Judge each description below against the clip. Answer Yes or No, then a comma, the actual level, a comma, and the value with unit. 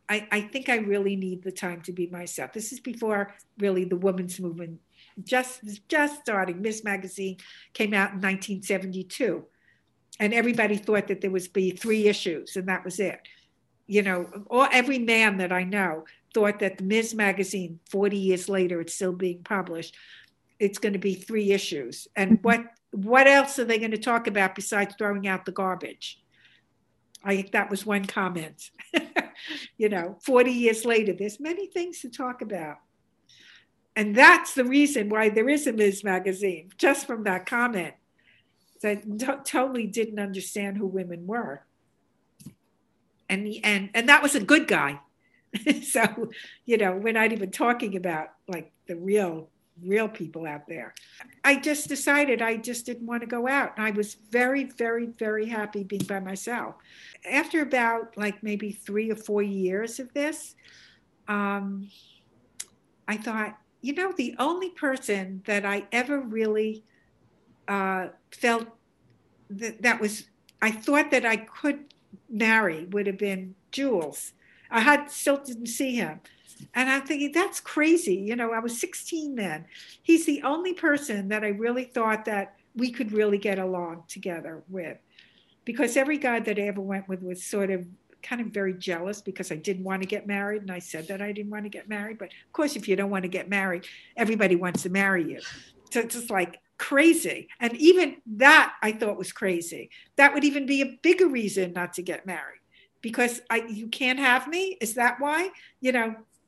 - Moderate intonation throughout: Yes, average, 4.2 semitones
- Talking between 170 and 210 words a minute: Yes, average, 175 wpm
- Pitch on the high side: Yes, high, 210 Hz